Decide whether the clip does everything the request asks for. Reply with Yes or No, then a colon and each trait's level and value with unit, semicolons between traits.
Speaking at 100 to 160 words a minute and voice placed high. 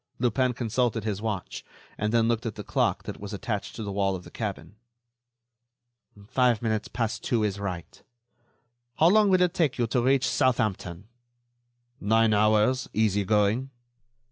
No: average, 155 wpm; low, 110 Hz